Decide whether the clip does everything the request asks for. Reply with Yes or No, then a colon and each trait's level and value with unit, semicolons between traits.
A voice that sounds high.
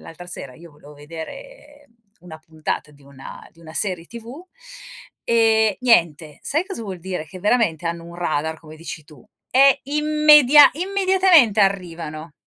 No: medium, 180 Hz